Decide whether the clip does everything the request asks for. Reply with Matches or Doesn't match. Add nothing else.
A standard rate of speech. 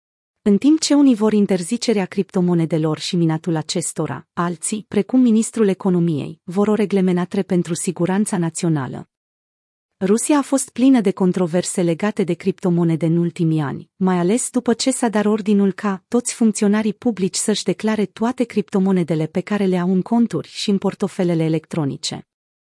Matches